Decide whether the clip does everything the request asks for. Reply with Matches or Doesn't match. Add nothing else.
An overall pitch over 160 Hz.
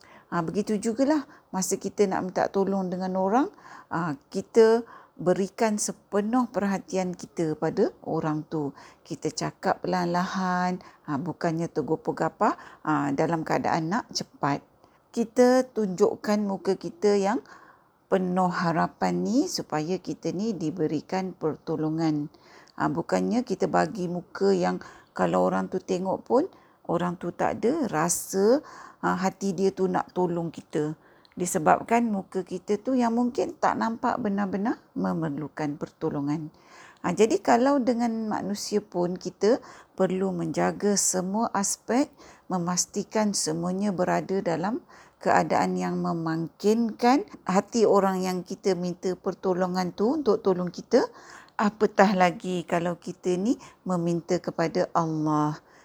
Matches